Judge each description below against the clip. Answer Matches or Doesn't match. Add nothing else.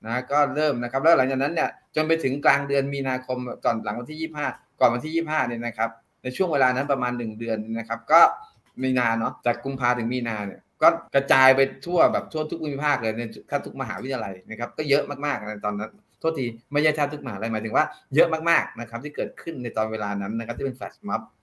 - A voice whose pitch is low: Matches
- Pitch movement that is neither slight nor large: Matches